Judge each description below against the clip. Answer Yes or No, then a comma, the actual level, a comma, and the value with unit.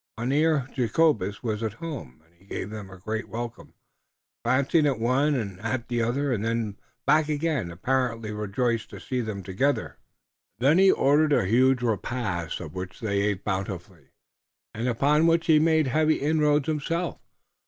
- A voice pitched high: No, low, 120 Hz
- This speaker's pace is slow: No, average, 165 wpm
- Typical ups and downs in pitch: No, wide, 5.8 semitones